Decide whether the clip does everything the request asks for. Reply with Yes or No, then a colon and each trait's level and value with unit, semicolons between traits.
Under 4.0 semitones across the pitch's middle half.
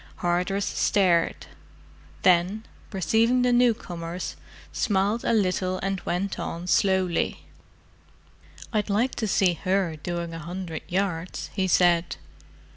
Yes: narrow, 2.5 semitones